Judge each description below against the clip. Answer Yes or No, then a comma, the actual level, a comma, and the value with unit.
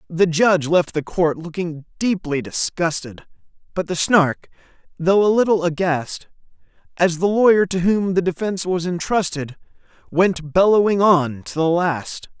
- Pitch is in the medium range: Yes, medium, 175 Hz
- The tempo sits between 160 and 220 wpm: No, average, 145 wpm